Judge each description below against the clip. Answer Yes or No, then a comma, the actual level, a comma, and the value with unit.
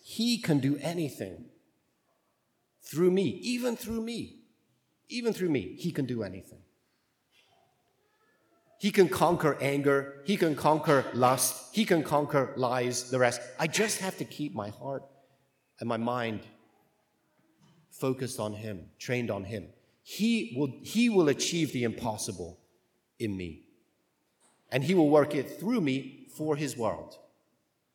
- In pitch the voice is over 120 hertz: Yes, medium, 140 Hz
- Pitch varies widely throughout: Yes, wide, 5.9 semitones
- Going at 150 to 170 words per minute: No, average, 140 wpm